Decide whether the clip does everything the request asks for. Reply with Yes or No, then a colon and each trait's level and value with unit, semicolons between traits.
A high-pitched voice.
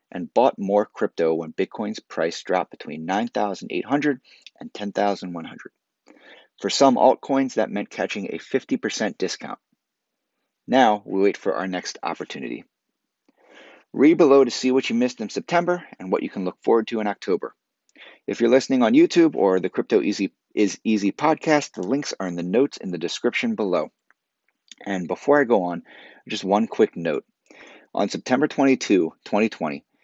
No: low, 120 Hz